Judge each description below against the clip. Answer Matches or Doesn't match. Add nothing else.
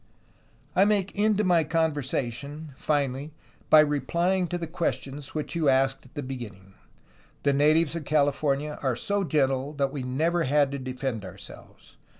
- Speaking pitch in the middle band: Matches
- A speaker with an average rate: Matches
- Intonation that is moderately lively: Matches